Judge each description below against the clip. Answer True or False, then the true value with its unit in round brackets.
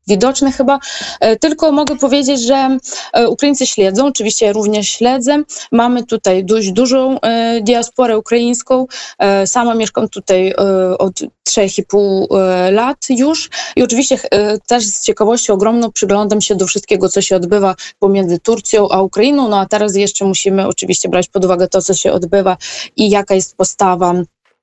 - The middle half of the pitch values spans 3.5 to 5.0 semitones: True (4.1 semitones)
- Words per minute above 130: True (145 wpm)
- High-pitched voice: True (215 Hz)